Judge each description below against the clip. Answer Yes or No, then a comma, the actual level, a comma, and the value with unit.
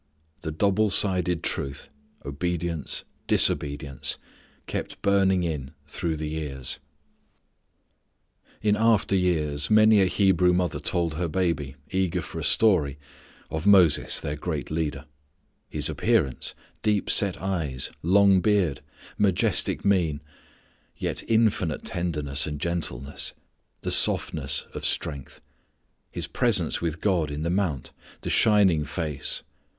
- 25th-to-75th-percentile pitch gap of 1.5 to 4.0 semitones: No, average, 4.4 semitones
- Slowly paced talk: Yes, slow, 120 wpm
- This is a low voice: Yes, very low, 85 Hz